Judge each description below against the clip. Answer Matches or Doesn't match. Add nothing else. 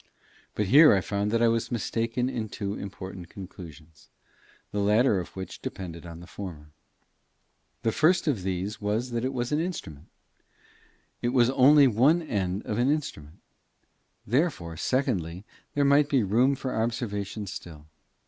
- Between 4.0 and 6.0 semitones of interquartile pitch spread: Matches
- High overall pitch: Doesn't match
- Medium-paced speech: Matches